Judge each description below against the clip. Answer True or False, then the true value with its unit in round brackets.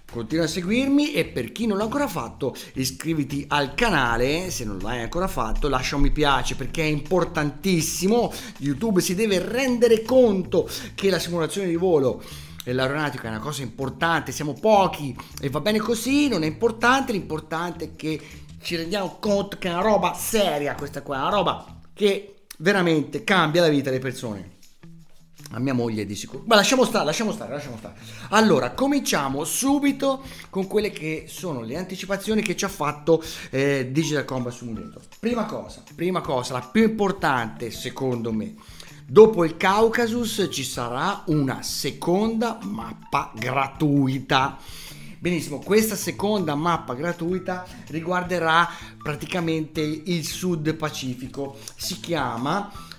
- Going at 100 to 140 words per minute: False (150 wpm)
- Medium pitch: True (165 Hz)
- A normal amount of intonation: False (6.6 semitones)